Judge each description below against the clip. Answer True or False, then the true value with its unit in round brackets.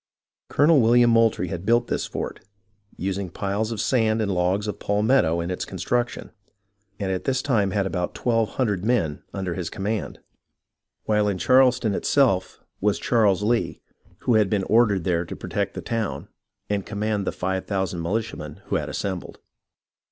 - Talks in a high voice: False (105 Hz)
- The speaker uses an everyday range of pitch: True (3.4 semitones)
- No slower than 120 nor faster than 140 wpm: False (165 wpm)